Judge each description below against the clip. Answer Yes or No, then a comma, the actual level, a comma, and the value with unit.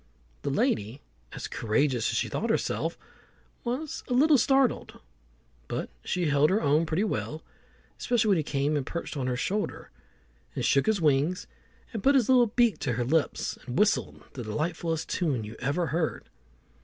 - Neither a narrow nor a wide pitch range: No, wide, 7.7 semitones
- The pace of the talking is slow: No, average, 170 wpm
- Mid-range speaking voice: Yes, medium, 160 Hz